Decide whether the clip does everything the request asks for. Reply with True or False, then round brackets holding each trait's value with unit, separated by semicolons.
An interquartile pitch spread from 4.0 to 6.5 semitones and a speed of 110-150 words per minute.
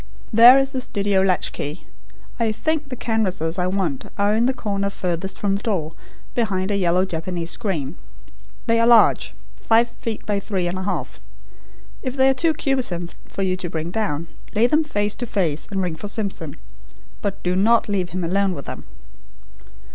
False (4.3 semitones; 185 wpm)